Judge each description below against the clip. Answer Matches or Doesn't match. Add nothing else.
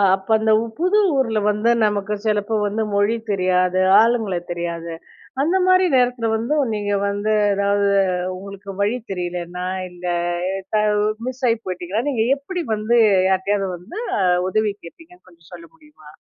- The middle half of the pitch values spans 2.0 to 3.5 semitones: Doesn't match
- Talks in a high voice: Matches